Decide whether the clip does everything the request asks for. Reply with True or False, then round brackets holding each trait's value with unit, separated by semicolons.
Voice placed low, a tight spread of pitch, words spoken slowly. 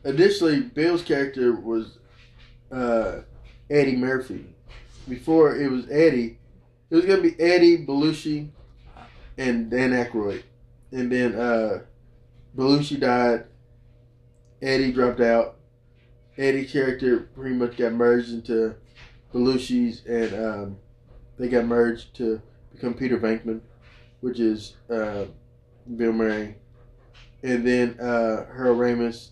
True (120 Hz; 1.4 semitones; 115 wpm)